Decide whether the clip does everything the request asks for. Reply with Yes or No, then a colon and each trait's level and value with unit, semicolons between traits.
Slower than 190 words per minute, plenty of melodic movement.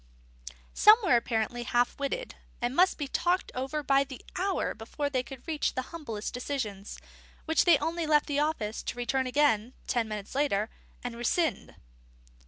No: average, 165 wpm; average, 4.3 semitones